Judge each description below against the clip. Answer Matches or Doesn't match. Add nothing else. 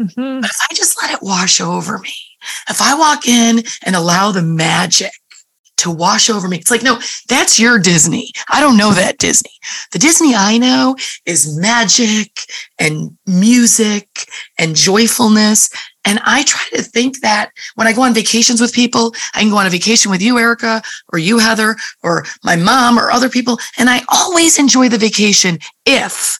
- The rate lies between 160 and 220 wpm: Matches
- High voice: Matches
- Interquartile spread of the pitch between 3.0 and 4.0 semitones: Matches